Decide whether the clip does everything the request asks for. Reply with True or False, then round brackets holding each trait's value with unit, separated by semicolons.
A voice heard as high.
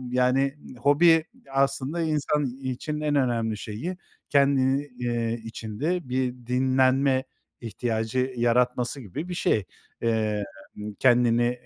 False (130 Hz)